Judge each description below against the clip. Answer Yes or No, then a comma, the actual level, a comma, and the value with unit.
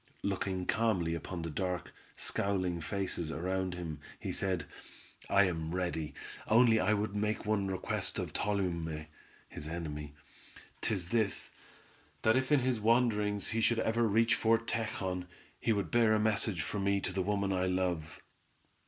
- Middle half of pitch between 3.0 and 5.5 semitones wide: Yes, average, 3.6 semitones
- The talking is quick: No, average, 155 wpm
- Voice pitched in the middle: No, low, 100 Hz